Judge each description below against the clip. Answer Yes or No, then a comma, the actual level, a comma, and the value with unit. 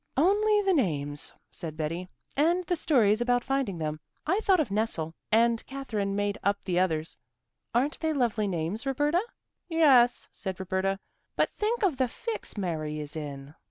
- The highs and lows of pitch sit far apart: Yes, wide, 9.0 semitones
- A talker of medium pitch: No, high, 220 Hz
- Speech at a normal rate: Yes, average, 160 wpm